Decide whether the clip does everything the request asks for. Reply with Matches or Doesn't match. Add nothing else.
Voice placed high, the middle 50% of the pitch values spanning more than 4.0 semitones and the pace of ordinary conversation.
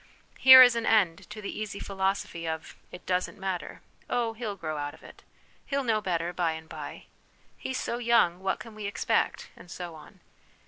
Doesn't match